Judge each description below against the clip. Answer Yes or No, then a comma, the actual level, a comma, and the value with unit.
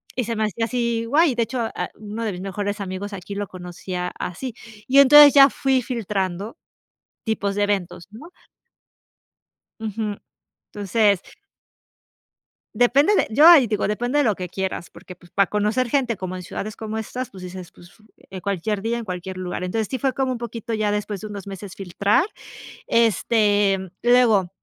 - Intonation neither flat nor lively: Yes, average, 3.8 semitones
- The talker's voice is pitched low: No, high, 210 Hz